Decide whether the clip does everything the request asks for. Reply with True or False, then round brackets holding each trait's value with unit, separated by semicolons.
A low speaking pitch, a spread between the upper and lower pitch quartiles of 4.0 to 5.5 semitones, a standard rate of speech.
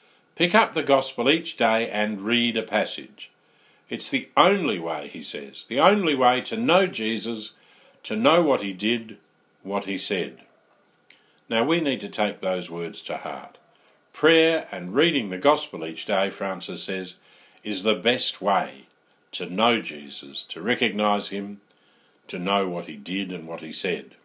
True (105 Hz; 4.6 semitones; 165 wpm)